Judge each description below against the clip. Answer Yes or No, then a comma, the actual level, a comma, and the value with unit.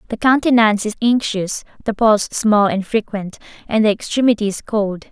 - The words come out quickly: No, average, 150 wpm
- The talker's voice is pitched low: No, high, 215 Hz